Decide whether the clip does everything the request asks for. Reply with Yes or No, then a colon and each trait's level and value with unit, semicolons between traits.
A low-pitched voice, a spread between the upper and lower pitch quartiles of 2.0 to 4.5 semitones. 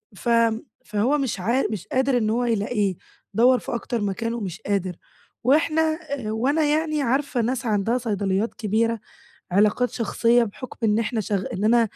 No: high, 230 Hz; average, 3.6 semitones